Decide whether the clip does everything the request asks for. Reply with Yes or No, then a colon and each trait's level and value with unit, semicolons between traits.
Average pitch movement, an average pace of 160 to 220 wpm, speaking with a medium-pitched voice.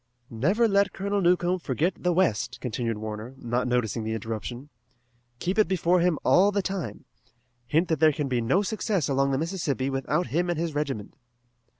No: wide, 6.6 semitones; average, 180 wpm; medium, 155 Hz